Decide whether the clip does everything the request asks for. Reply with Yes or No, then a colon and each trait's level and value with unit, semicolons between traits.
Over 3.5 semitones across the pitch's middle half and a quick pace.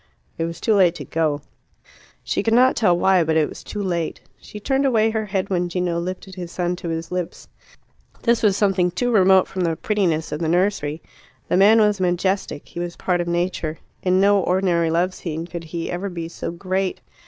No: narrow, 2.6 semitones; fast, 210 wpm